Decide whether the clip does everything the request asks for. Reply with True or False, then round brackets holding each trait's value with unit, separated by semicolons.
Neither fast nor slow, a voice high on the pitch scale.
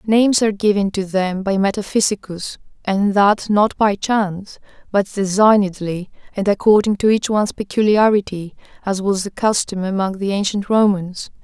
True (145 wpm; 200 Hz)